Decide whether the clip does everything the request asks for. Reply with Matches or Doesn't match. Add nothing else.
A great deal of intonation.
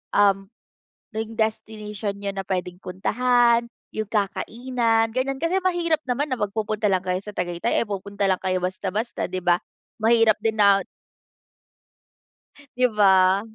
Doesn't match